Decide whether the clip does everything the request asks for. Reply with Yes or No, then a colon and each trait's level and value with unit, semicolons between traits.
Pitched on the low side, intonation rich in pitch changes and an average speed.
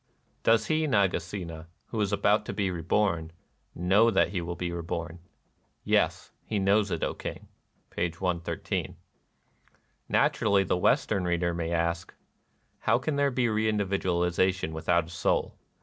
No: very low, 90 Hz; average, 3.6 semitones; average, 160 wpm